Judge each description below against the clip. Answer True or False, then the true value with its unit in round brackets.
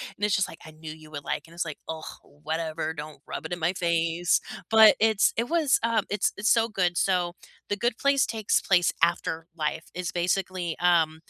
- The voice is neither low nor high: True (175 Hz)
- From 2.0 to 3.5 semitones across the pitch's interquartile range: False (4.4 semitones)